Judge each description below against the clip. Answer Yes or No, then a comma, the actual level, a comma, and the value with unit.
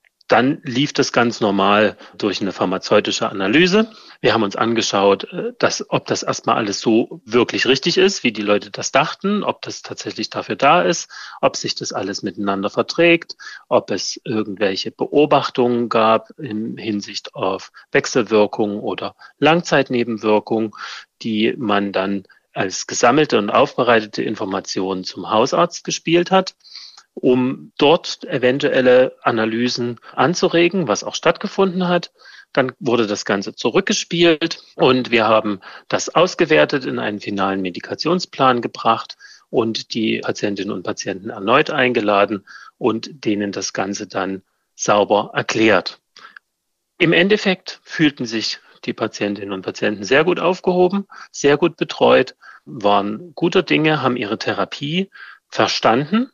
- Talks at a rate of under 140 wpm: Yes, average, 130 wpm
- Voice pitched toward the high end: No, low, 125 Hz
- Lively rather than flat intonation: Yes, wide, 8.6 semitones